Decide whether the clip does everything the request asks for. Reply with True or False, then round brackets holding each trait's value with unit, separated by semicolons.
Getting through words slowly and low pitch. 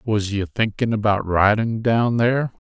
False (155 wpm; 110 Hz)